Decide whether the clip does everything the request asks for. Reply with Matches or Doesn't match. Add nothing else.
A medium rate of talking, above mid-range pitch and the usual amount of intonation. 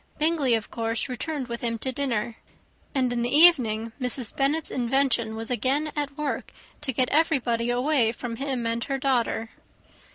Matches